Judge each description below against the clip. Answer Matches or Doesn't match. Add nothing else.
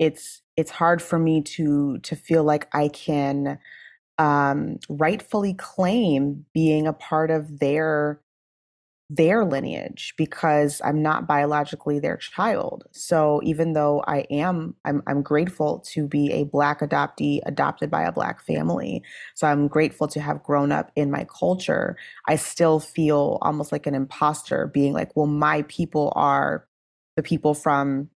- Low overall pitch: Doesn't match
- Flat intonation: Matches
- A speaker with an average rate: Matches